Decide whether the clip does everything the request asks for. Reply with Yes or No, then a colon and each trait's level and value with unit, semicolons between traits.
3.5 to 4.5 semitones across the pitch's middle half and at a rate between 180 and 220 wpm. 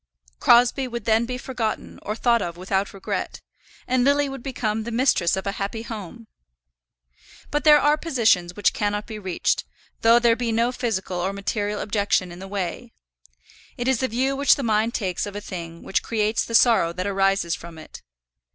Yes: average, 3.9 semitones; average, 190 wpm